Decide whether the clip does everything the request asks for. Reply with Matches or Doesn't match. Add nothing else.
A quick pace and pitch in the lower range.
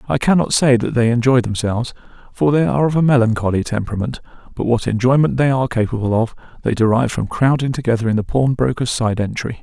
Doesn't match